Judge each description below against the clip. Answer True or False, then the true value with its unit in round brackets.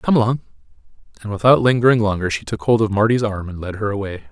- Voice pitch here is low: True (105 Hz)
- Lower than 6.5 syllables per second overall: False (6.8 syllables/s)